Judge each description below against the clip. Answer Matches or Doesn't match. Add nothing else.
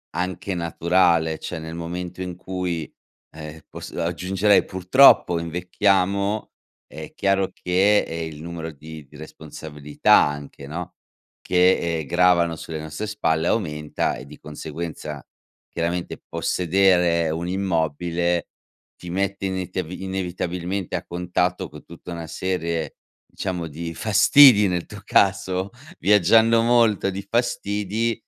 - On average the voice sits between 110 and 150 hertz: Doesn't match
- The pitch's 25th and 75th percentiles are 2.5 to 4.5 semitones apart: Matches